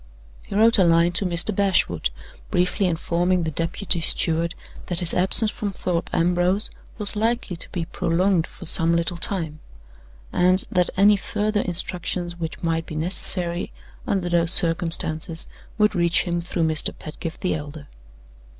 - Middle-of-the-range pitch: Yes, medium, 175 Hz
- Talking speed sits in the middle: Yes, average, 150 wpm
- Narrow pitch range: Yes, narrow, 2.3 semitones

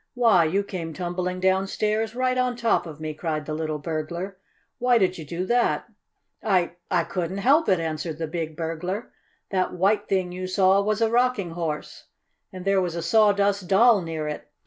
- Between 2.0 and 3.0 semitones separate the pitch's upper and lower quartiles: No, average, 3.9 semitones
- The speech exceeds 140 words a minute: Yes, average, 185 wpm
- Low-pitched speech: No, medium, 185 Hz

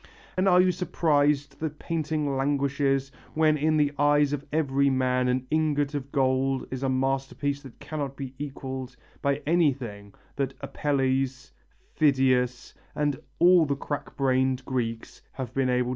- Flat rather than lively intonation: Yes, narrow, 2.0 semitones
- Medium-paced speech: Yes, average, 155 wpm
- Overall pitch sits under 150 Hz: Yes, medium, 140 Hz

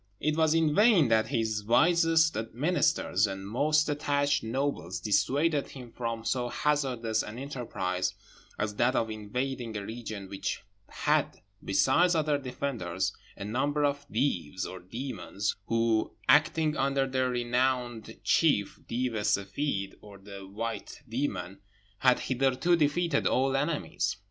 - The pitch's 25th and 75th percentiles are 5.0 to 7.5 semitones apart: Yes, average, 5.3 semitones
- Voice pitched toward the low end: Yes, low, 125 Hz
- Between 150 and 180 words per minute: No, slow, 135 wpm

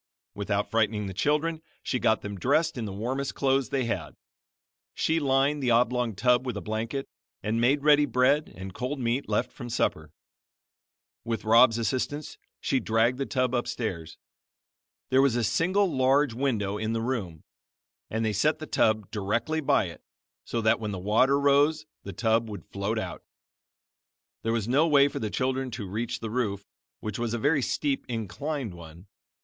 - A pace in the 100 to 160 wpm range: No, average, 175 wpm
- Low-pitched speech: Yes, low, 120 Hz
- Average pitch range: Yes, average, 4.3 semitones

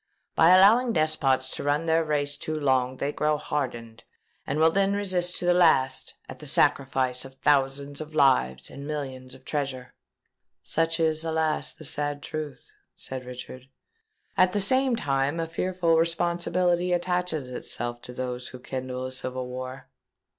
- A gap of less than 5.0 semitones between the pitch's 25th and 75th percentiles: Yes, average, 4.2 semitones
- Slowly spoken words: No, average, 160 wpm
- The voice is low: No, medium, 145 Hz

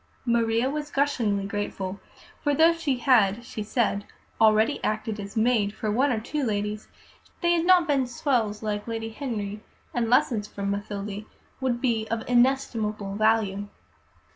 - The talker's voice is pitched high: Yes, high, 225 Hz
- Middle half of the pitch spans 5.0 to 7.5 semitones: No, average, 3.7 semitones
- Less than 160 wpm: Yes, average, 150 wpm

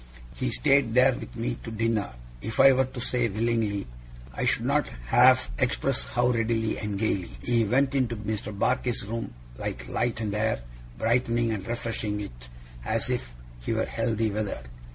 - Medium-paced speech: Yes, average, 170 wpm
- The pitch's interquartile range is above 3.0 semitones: No, average, 2.7 semitones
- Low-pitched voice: Yes, low, 115 Hz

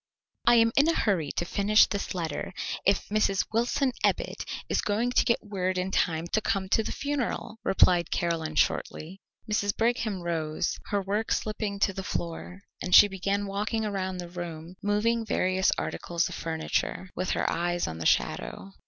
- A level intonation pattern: No, average, 3.5 semitones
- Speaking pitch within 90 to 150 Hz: No, high, 195 Hz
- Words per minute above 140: Yes, average, 175 wpm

